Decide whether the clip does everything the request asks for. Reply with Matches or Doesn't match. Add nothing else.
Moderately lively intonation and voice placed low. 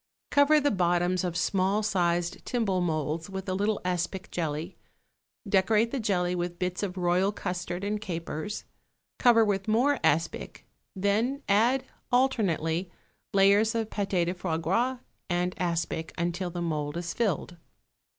Doesn't match